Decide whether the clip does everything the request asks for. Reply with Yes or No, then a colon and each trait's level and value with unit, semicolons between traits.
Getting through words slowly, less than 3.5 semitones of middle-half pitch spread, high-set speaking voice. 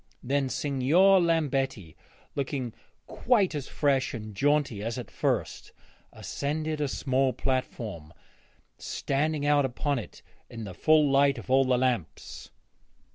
No: slow, 130 wpm; average, 2.9 semitones; low, 135 Hz